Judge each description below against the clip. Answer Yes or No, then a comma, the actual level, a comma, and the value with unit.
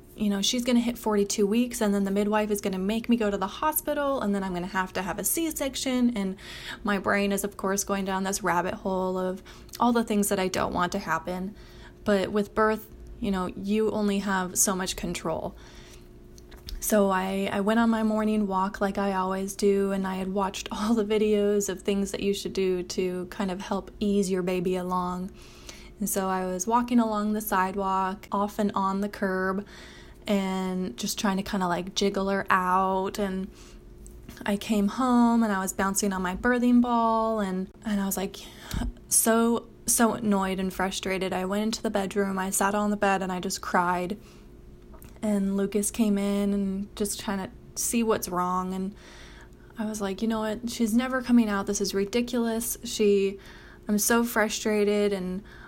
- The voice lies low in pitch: No, high, 200 Hz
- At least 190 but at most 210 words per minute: Yes, average, 200 wpm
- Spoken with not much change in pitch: Yes, narrow, 2.2 semitones